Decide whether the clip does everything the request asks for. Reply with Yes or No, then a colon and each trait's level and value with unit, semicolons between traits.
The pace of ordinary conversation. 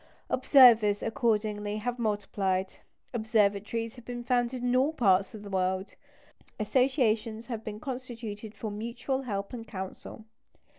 No: slow, 130 wpm